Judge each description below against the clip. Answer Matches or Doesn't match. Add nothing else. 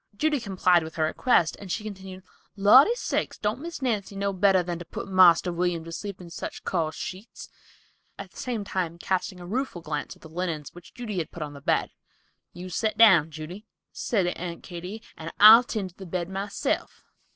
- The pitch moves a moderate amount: Matches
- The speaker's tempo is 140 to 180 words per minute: Doesn't match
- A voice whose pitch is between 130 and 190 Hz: Matches